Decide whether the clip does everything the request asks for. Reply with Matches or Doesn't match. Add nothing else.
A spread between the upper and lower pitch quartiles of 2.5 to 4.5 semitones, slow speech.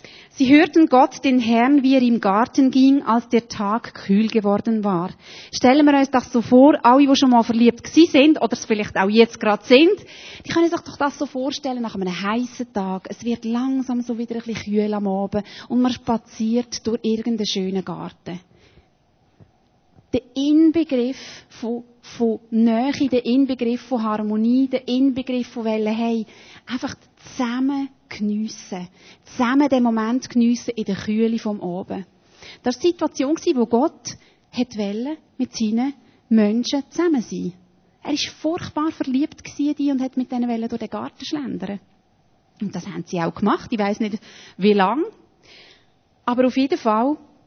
Doesn't match